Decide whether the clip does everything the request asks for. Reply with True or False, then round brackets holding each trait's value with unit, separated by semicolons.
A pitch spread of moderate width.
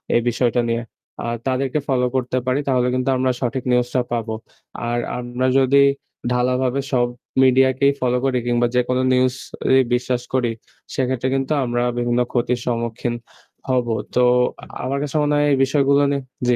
False (1.4 semitones)